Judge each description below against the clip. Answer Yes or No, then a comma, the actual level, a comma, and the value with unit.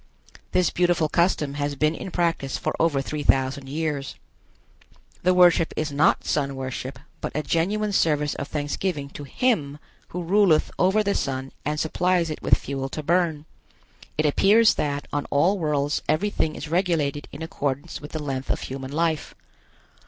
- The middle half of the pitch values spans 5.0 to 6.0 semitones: No, average, 3.6 semitones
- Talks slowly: No, average, 165 wpm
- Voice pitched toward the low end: No, medium, 155 Hz